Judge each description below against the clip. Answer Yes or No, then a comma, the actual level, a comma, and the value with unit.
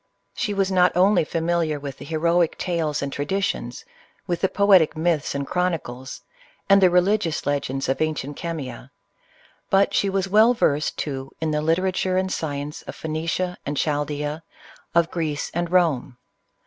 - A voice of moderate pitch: Yes, medium, 165 Hz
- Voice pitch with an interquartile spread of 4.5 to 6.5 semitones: No, average, 3.9 semitones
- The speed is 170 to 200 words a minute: No, average, 155 wpm